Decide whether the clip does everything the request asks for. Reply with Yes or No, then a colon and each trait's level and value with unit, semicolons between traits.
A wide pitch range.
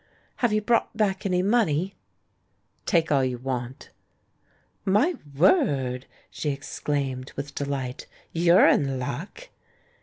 Yes: wide, 6.8 semitones